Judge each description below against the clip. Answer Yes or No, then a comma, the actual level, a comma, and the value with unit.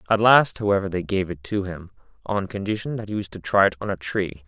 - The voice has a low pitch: Yes, very low, 95 Hz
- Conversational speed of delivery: No, fast, 255 wpm